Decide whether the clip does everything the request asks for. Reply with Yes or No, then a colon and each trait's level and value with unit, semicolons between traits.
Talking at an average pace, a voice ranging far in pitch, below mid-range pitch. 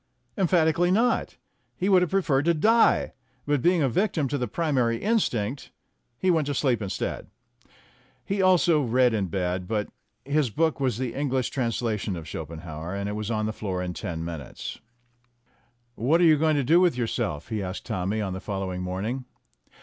Yes: average, 180 wpm; wide, 8.3 semitones; low, 125 Hz